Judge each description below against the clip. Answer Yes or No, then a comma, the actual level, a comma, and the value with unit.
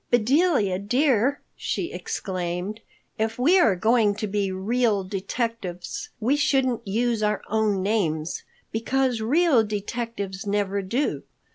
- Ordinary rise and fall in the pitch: Yes, average, 3.9 semitones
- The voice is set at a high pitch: Yes, high, 220 Hz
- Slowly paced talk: Yes, slow, 120 wpm